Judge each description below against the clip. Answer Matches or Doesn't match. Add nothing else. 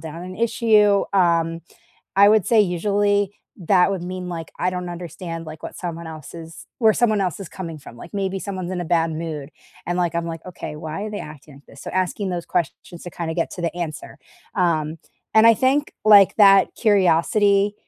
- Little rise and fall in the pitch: Doesn't match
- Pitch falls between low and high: Matches